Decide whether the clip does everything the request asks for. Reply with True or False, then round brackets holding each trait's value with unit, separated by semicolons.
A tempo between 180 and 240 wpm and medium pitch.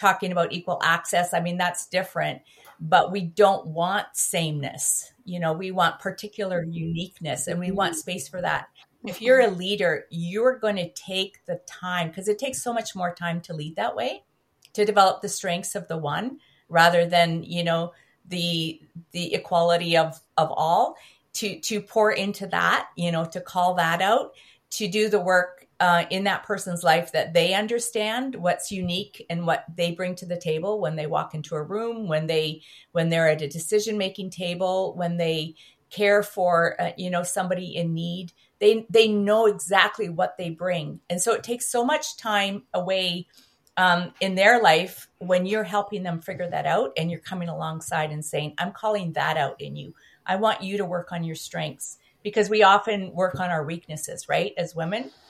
True (190 wpm; 180 Hz)